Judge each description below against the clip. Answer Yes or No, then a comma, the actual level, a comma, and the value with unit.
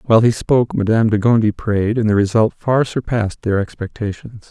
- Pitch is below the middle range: Yes, low, 110 Hz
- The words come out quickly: No, average, 185 wpm